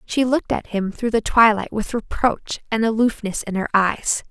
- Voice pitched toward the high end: Yes, high, 220 Hz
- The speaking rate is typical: Yes, average, 195 wpm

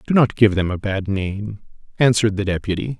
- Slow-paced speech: No, average, 200 wpm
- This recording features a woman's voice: No, male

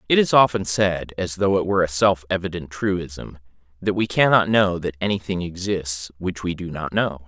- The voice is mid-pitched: No, very low, 90 Hz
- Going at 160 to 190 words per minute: No, average, 200 wpm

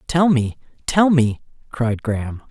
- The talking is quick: No, average, 145 wpm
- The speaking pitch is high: No, low, 135 Hz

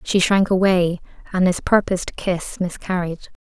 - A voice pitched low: No, medium, 180 Hz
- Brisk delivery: No, average, 140 wpm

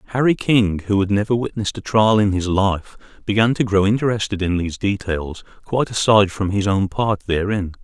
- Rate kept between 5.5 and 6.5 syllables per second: Yes, 5.6 syllables/s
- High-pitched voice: No, low, 100 Hz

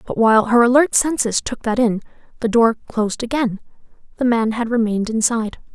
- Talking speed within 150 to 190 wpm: Yes, average, 165 wpm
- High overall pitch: Yes, high, 230 Hz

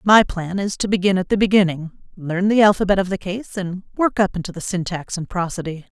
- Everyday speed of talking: No, fast, 220 wpm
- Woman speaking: Yes, female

